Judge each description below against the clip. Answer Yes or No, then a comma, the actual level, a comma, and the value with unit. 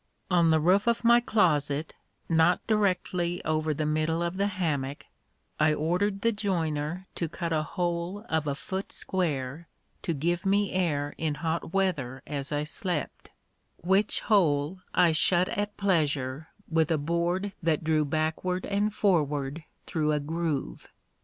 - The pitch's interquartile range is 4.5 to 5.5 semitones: No, average, 3.5 semitones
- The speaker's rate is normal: Yes, average, 150 wpm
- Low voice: No, medium, 165 Hz